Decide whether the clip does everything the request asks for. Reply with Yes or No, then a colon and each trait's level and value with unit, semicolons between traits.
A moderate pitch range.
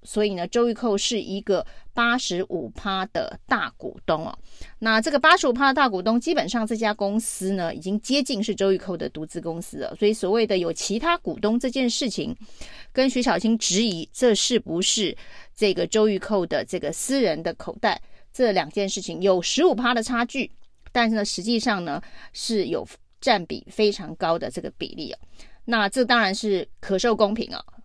Yes: average, 3.7 semitones